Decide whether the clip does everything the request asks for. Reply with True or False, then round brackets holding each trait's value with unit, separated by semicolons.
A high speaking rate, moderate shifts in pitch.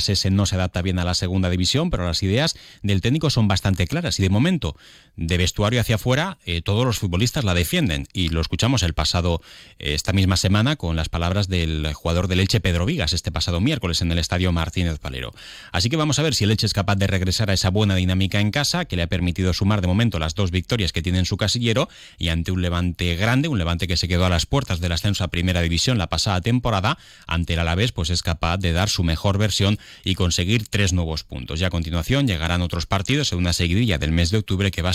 True (240 wpm; 3.5 semitones)